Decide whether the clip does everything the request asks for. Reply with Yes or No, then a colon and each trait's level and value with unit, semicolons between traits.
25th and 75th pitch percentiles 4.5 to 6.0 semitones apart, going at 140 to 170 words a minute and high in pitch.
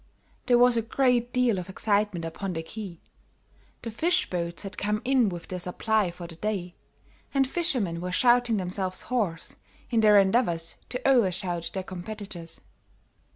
Yes: average, 5.1 semitones; average, 160 wpm; high, 200 Hz